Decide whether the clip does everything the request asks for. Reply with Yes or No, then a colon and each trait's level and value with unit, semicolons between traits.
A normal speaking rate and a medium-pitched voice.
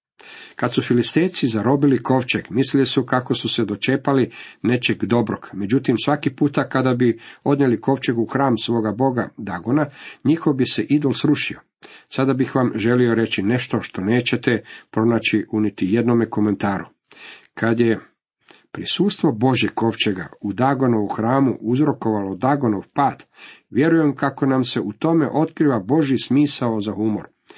No: average, 140 wpm; low, 125 Hz